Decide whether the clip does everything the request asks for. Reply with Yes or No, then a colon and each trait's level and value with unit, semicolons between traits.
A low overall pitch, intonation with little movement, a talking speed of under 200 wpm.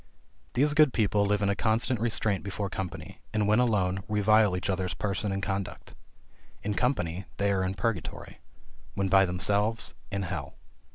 Yes: low, 100 Hz; narrow, 2.2 semitones; average, 165 wpm